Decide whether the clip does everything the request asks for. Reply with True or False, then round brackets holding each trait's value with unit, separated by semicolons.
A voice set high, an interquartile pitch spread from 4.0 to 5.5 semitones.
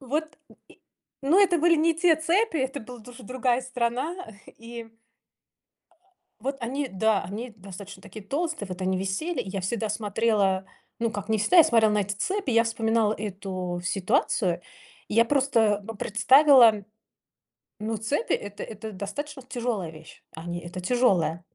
True (225 Hz; 5.0 semitones)